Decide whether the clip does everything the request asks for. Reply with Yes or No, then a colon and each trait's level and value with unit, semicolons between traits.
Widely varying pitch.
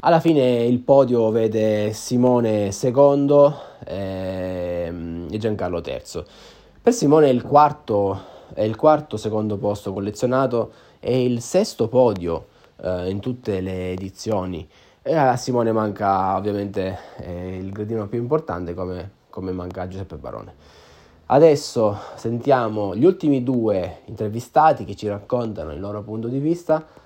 No: average, 4.9 semitones